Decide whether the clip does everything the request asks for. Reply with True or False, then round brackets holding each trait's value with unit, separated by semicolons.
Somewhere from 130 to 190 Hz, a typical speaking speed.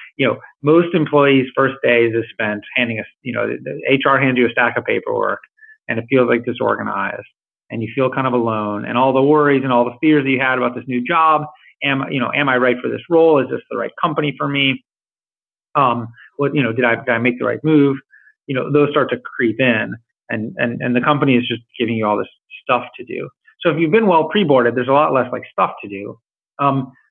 False (135 Hz; 250 wpm)